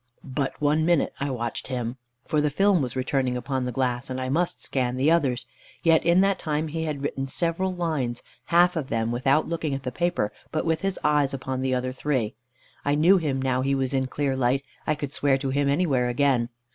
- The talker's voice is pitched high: No, medium, 140 Hz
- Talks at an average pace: No, fast, 220 wpm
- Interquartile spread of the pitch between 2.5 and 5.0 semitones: Yes, average, 3.6 semitones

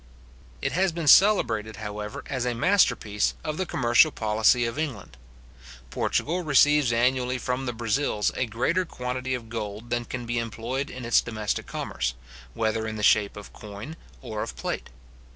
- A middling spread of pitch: Yes, average, 3.6 semitones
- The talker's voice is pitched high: No, low, 120 Hz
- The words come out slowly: No, average, 165 wpm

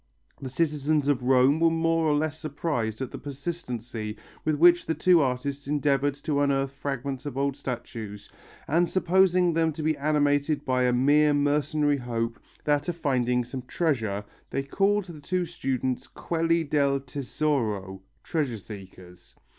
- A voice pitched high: No, medium, 145 Hz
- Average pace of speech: Yes, average, 155 wpm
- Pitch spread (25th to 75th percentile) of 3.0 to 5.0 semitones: Yes, average, 3.8 semitones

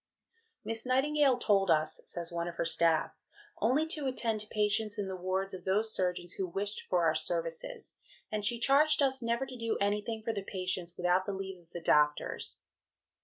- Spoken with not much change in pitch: No, average, 4.7 semitones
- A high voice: Yes, high, 200 Hz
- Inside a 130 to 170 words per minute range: No, average, 190 wpm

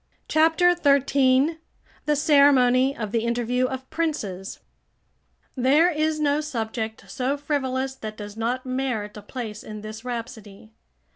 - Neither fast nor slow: No, slow, 130 wpm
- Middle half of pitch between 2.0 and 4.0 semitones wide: No, average, 4.4 semitones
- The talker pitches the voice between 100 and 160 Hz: No, very high, 255 Hz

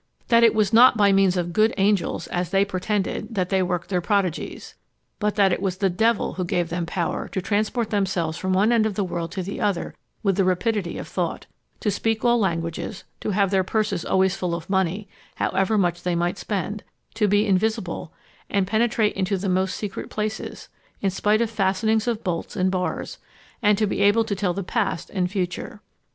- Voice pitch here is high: Yes, high, 195 Hz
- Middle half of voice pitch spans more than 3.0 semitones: No, average, 2.7 semitones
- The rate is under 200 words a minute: No, fast, 205 wpm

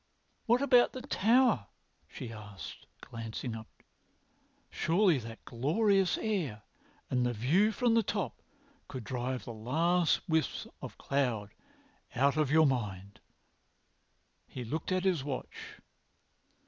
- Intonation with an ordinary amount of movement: No, wide, 8.6 semitones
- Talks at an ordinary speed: No, slow, 120 wpm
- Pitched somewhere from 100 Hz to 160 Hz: Yes, medium, 140 Hz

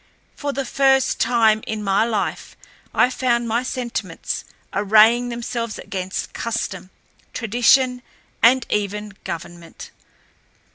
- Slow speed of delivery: Yes, slow, 105 wpm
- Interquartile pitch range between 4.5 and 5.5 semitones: No, average, 2.9 semitones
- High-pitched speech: Yes, high, 230 Hz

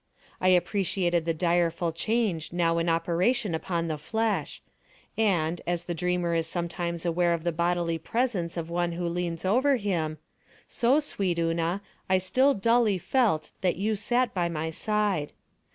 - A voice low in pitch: No, medium, 175 Hz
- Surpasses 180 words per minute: No, average, 155 wpm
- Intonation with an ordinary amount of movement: Yes, average, 3.4 semitones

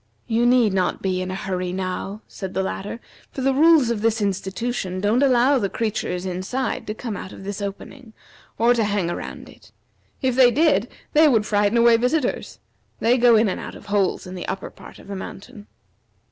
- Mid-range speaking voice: No, high, 215 Hz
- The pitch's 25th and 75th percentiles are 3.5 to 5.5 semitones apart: Yes, average, 4.2 semitones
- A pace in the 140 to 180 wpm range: No, average, 200 wpm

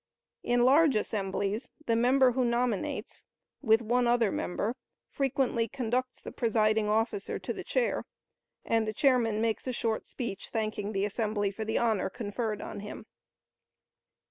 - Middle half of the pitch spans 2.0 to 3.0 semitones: Yes, narrow, 2.6 semitones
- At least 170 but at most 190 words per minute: No, average, 145 wpm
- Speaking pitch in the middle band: No, high, 225 Hz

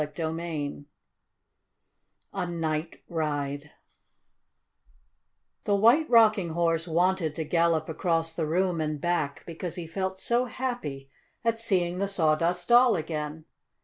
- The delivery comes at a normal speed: No, slow, 120 wpm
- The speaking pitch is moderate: Yes, medium, 170 Hz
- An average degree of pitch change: Yes, average, 3.3 semitones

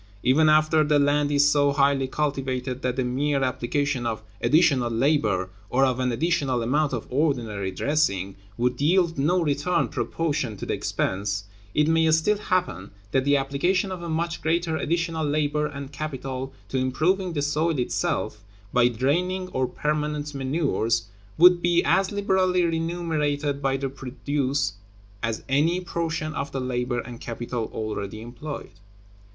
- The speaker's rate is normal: Yes, average, 150 wpm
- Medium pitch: Yes, medium, 145 Hz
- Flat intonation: No, average, 4.1 semitones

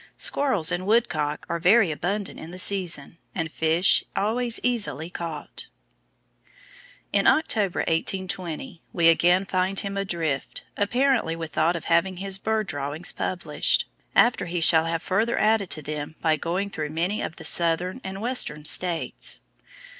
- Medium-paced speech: Yes, average, 145 wpm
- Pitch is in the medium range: Yes, medium, 180 Hz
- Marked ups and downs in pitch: No, average, 3.7 semitones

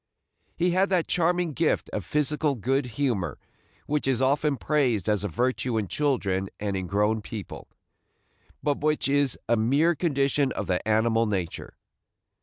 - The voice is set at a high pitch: No, low, 130 Hz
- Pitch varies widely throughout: Yes, wide, 5.9 semitones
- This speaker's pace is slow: No, average, 155 wpm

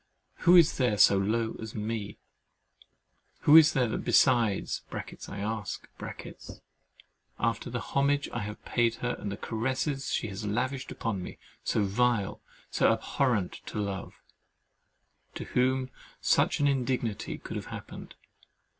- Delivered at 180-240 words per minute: No, slow, 135 wpm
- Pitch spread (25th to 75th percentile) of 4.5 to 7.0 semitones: No, average, 4.0 semitones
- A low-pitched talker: Yes, low, 115 Hz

